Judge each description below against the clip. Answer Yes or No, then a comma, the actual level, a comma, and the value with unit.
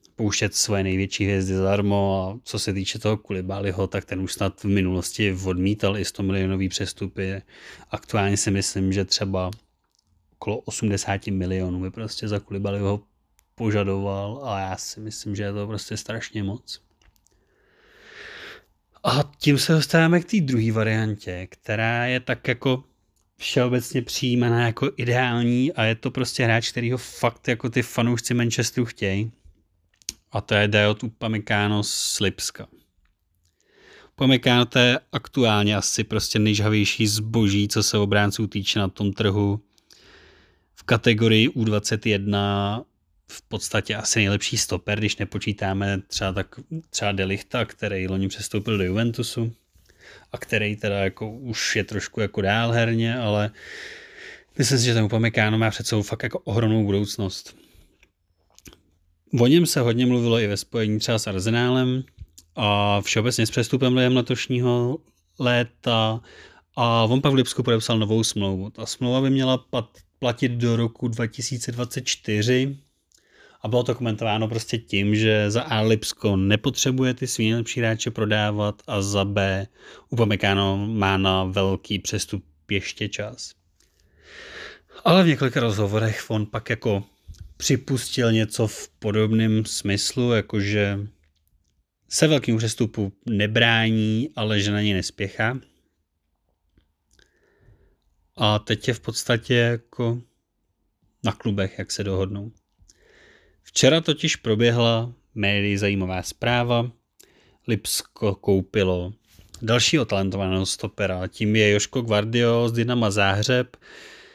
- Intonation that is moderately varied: Yes, average, 3.3 semitones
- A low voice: Yes, low, 110 Hz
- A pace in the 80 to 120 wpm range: No, average, 130 wpm